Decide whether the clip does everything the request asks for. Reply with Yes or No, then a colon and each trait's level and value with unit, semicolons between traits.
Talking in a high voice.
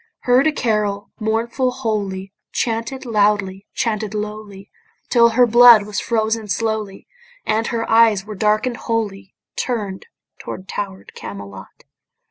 Yes: high, 215 Hz